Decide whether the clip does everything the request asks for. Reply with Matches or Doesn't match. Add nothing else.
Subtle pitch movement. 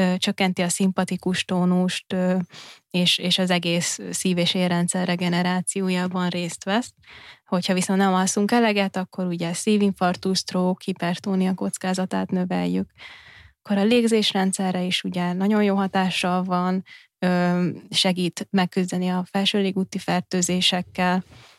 Matches